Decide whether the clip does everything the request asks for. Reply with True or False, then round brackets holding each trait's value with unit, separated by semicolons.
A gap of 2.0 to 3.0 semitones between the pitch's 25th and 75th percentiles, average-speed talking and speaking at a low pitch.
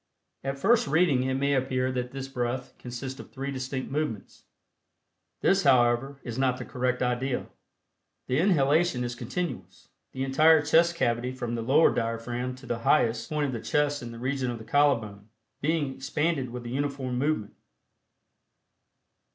True (2.7 semitones; 165 wpm; 130 Hz)